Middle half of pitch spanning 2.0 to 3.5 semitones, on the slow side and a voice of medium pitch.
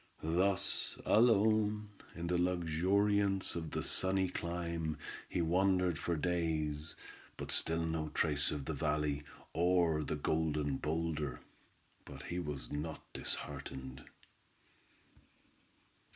No: average, 3.2 semitones; slow, 110 wpm; very low, 80 Hz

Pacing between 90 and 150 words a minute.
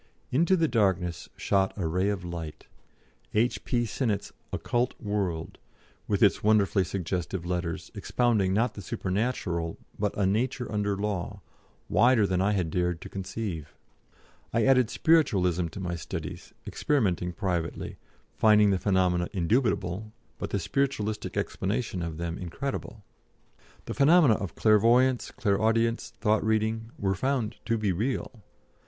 Yes: slow, 135 wpm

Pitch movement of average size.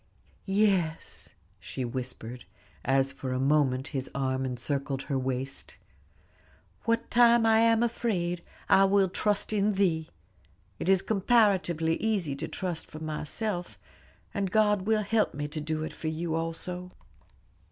No: wide, 6.7 semitones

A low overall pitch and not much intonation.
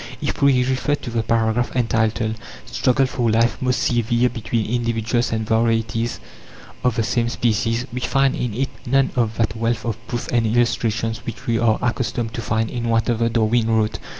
Yes: low, 115 Hz; narrow, 1.3 semitones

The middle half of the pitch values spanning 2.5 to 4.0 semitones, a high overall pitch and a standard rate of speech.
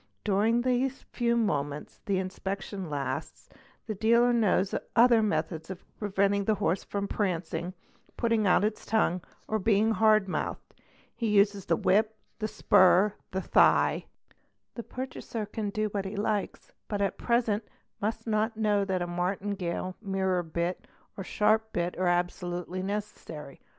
Yes: average, 3.0 semitones; high, 200 Hz; average, 145 wpm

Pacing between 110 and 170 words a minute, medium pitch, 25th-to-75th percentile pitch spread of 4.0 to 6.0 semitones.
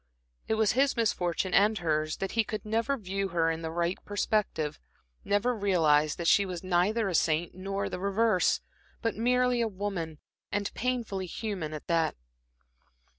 No: average, 165 wpm; high, 195 Hz; average, 4.4 semitones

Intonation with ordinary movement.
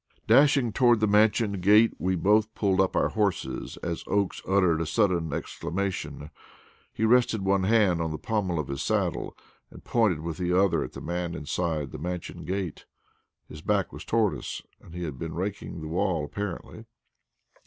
Yes: average, 4.0 semitones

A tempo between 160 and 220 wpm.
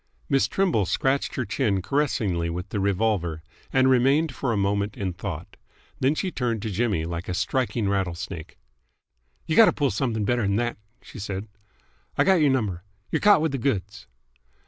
Yes: average, 175 wpm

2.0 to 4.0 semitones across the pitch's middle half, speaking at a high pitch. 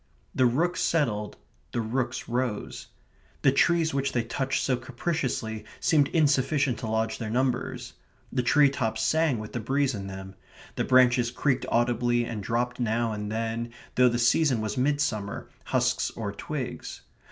No: average, 3.3 semitones; low, 120 Hz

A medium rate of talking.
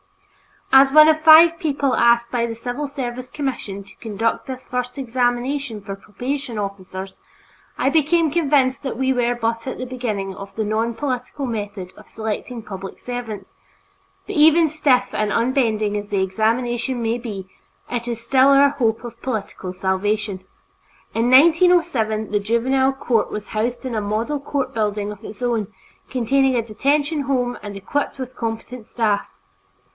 Yes: average, 160 wpm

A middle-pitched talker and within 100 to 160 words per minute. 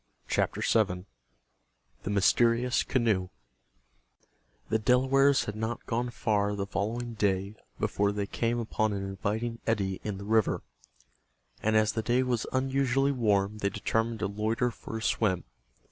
No: low, 110 Hz; average, 140 wpm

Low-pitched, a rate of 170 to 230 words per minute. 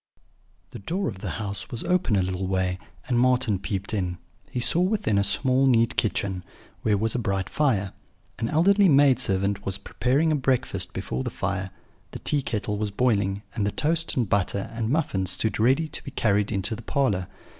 Yes: low, 110 Hz; average, 190 wpm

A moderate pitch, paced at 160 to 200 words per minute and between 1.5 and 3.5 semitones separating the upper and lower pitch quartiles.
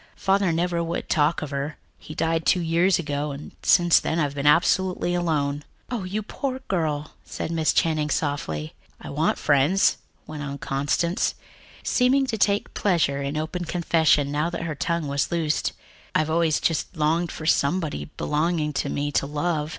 Yes: medium, 160 Hz; average, 175 wpm; average, 2.9 semitones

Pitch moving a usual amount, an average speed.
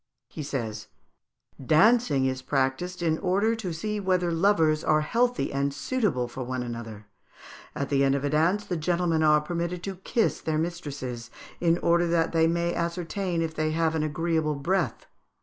Yes: average, 4.0 semitones; average, 170 wpm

